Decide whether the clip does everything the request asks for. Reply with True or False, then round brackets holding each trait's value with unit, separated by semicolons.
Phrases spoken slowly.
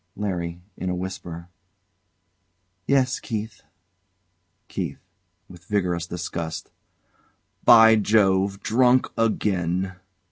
True (80 wpm)